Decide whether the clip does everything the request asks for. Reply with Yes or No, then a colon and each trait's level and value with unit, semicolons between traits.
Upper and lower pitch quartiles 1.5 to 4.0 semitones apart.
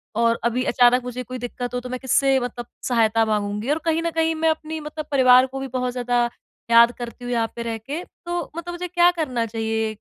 No: average, 4.6 semitones